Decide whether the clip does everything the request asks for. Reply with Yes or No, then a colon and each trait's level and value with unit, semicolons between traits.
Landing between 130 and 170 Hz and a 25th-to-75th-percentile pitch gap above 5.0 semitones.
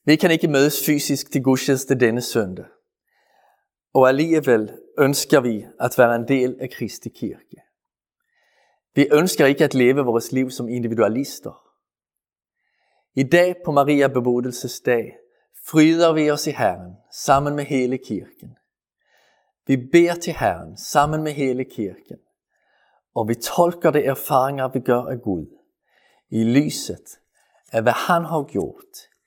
No: low, 135 Hz; average, 4.2 semitones